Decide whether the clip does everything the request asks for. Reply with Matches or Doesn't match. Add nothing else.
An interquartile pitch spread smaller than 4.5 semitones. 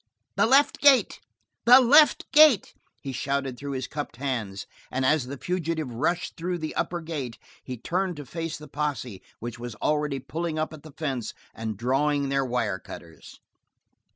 Doesn't match